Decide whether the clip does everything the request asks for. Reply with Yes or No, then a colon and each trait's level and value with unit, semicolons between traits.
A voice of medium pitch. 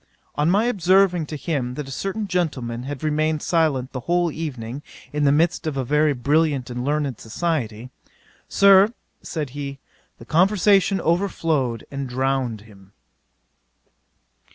Yes: medium, 150 Hz